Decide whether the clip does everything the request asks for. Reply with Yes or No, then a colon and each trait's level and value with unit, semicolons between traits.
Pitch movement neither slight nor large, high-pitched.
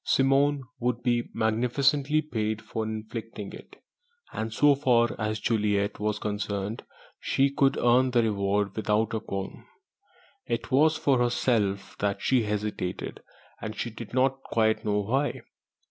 No: average, 3.6 semitones; low, 115 Hz